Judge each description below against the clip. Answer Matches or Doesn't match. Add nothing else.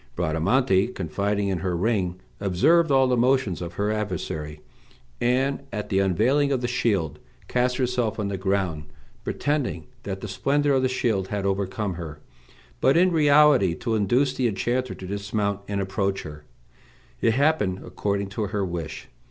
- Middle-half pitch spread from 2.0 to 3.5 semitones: Doesn't match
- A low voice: Matches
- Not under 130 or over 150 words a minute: Doesn't match